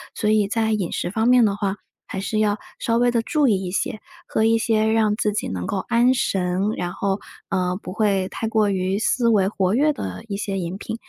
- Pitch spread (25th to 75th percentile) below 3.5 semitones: Yes, average, 2.7 semitones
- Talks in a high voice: Yes, high, 210 Hz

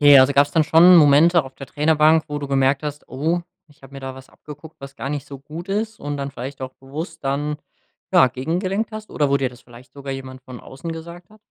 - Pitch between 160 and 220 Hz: No, medium, 145 Hz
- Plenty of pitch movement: No, average, 3.2 semitones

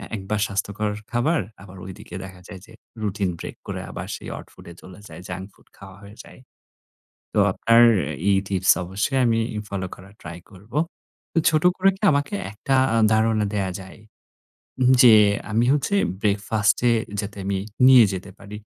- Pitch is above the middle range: No, low, 100 Hz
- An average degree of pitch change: Yes, average, 3.1 semitones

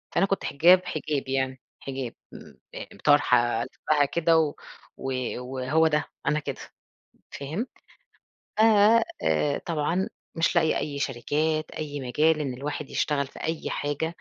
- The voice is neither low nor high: Yes, medium, 145 Hz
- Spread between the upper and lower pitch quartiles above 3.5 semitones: No, average, 3.1 semitones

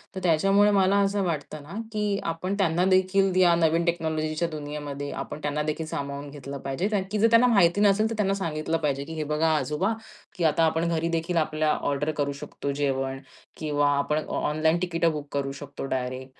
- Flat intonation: No, average, 4.2 semitones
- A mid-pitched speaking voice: Yes, medium, 160 Hz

